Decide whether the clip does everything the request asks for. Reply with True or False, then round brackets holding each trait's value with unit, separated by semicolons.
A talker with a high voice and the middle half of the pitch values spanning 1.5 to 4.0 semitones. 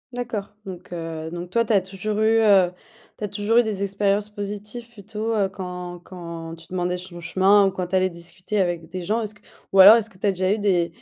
True (195 Hz; 2.8 semitones)